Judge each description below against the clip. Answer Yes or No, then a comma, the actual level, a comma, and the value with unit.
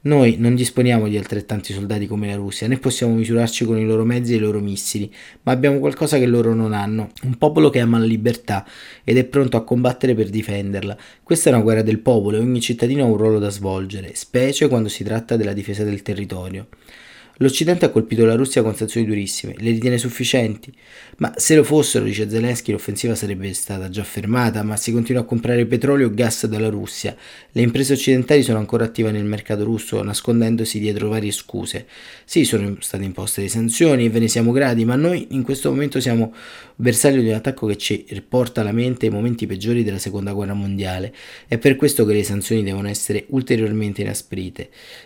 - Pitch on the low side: Yes, low, 115 Hz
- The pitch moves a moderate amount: Yes, average, 3.0 semitones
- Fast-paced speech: Yes, fast, 200 wpm